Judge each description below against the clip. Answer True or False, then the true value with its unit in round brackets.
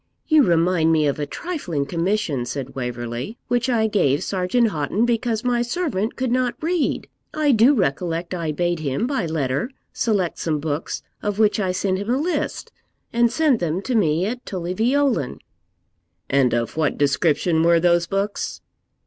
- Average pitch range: False (7.2 semitones)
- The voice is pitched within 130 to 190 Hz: True (185 Hz)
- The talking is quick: False (165 wpm)